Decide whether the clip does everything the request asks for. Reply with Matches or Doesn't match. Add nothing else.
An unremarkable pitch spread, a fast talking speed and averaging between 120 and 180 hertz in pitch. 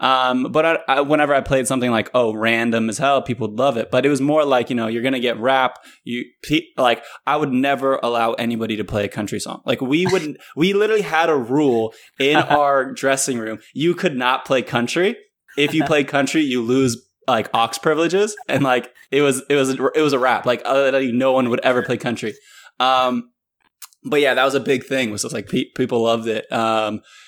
Matches